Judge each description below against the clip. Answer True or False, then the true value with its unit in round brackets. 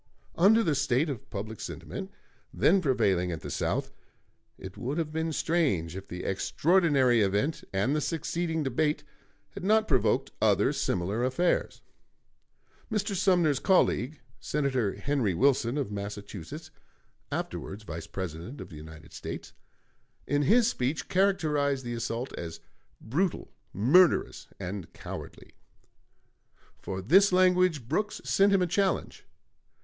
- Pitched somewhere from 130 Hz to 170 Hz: True (140 Hz)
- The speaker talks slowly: True (130 wpm)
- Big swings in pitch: True (8.8 semitones)